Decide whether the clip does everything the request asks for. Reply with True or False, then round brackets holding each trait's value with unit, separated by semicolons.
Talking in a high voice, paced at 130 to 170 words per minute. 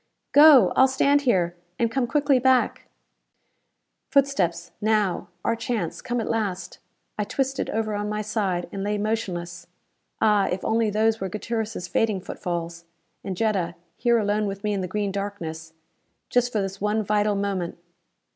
True (210 Hz; 155 wpm)